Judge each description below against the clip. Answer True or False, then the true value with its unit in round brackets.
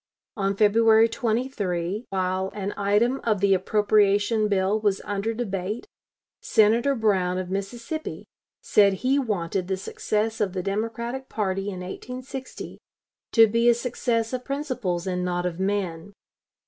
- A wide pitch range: False (3.3 semitones)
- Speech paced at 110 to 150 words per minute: True (135 wpm)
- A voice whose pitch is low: False (205 Hz)